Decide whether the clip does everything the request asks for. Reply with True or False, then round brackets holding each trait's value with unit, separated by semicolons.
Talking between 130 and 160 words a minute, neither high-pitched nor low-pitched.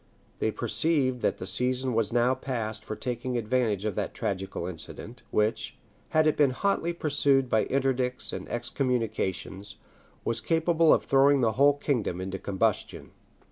False (150 wpm; 125 Hz)